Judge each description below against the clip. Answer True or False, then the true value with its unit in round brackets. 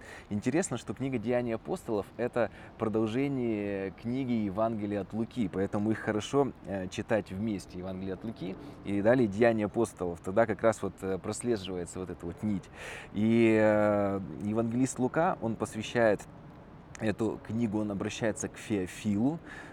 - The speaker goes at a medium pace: True (130 wpm)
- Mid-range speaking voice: False (110 Hz)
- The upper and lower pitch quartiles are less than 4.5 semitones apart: True (2.7 semitones)